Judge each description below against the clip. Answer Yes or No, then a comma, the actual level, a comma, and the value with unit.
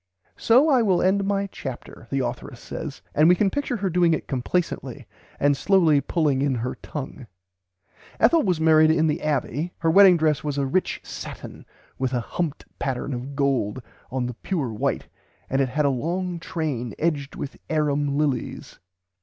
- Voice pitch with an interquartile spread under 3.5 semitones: No, average, 4.7 semitones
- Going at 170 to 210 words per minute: Yes, average, 180 wpm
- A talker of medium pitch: Yes, medium, 150 Hz